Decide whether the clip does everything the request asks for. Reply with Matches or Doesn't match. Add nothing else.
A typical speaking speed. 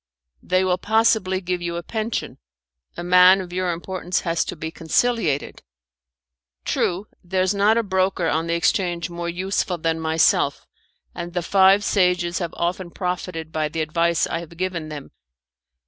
Matches